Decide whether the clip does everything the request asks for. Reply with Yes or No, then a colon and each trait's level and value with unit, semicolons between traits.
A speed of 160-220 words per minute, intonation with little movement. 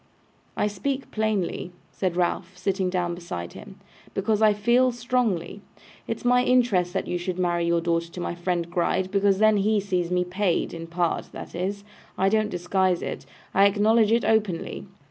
No: average, 175 wpm; average, 3.5 semitones